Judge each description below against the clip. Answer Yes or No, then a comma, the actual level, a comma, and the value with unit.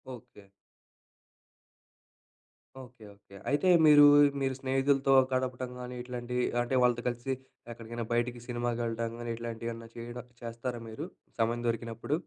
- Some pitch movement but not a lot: No, narrow, 1.6 semitones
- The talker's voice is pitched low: Yes, low, 120 Hz